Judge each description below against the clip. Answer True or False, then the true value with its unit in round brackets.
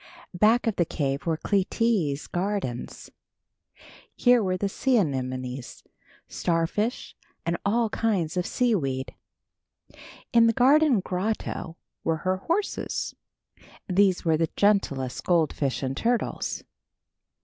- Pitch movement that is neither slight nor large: False (6.4 semitones)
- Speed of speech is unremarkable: False (110 wpm)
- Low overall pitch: False (185 Hz)